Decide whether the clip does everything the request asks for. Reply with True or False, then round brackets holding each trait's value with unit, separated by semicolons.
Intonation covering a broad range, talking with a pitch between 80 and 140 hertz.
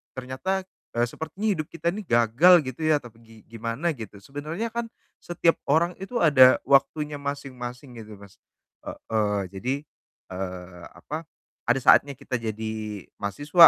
True (5.8 semitones; 135 Hz)